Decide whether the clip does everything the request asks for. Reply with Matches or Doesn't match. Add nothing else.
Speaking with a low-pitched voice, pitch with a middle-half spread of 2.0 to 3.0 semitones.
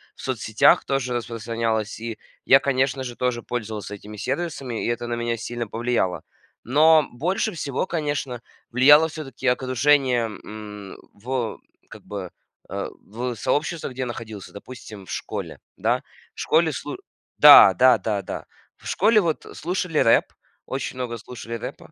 Doesn't match